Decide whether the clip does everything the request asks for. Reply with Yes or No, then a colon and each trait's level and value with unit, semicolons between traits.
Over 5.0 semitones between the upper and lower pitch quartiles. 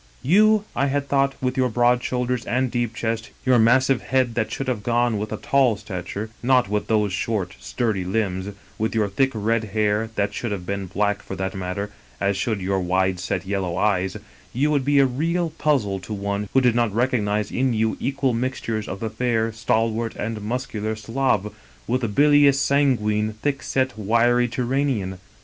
No: average, 3.9 semitones